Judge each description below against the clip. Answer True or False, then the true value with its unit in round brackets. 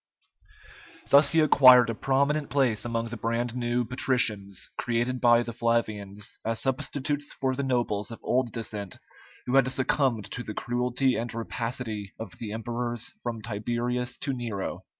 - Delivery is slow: False (150 wpm)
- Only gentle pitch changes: True (2.3 semitones)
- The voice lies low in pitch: True (120 Hz)